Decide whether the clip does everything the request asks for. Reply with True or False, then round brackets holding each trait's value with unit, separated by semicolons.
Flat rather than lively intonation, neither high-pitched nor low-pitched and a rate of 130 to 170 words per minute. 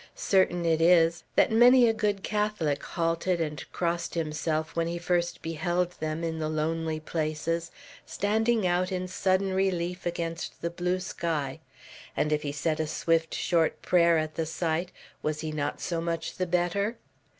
True (2.3 semitones; 170 Hz; 165 wpm)